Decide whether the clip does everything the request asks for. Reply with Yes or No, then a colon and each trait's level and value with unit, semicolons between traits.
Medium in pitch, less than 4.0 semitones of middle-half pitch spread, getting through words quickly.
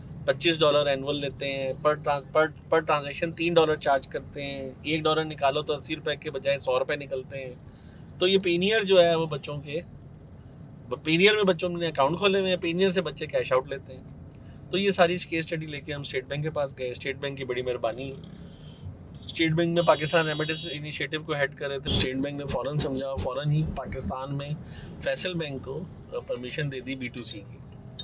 Yes: medium, 145 Hz; average, 3.3 semitones; fast, 210 wpm